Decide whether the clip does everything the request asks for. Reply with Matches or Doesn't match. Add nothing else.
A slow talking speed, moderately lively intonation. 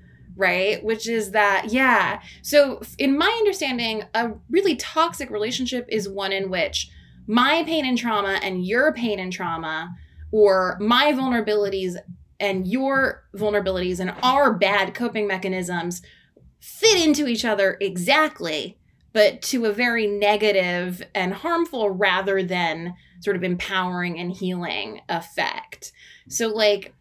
Matches